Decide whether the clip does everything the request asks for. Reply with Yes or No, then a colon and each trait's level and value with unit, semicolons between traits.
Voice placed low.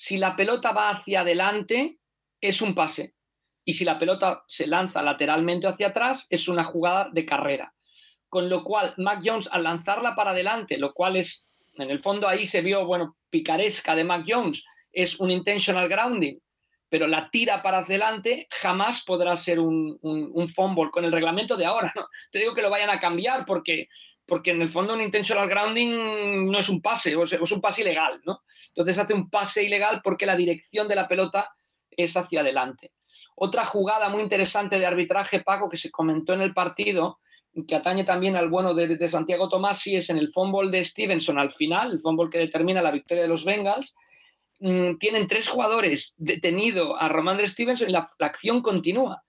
No: high, 190 Hz